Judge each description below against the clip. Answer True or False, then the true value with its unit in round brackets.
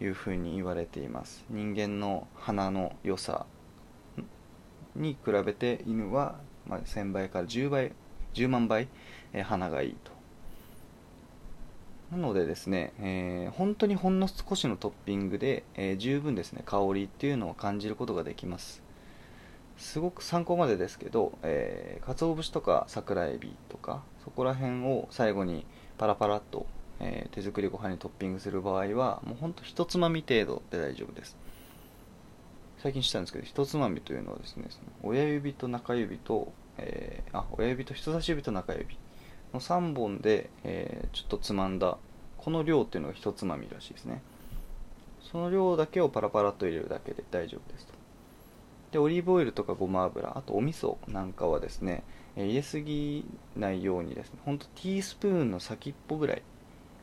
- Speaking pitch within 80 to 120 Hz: True (110 Hz)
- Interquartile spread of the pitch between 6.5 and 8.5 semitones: True (7.3 semitones)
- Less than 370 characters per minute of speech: True (325 characters per minute)